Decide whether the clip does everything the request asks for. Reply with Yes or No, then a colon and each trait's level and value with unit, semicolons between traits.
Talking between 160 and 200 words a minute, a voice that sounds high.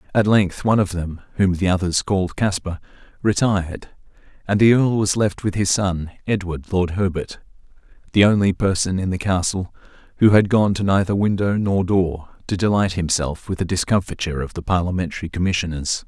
No: average, 170 wpm; very low, 95 Hz